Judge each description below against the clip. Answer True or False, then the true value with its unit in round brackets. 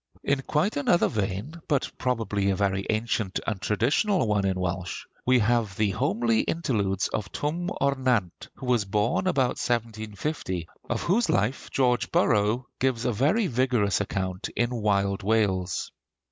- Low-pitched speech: True (110 Hz)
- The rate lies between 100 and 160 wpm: True (150 wpm)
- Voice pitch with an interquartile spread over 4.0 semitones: True (4.8 semitones)